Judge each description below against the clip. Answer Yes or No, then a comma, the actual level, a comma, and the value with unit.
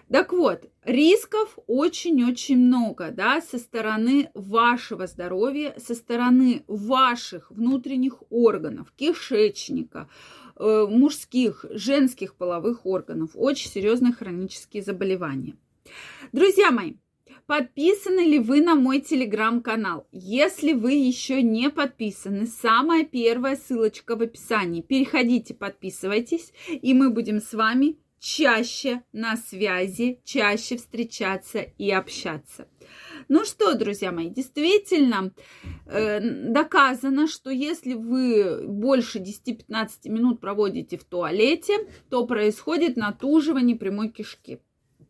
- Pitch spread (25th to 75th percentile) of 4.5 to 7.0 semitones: Yes, average, 4.8 semitones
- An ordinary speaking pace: No, slow, 100 wpm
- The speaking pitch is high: Yes, high, 245 Hz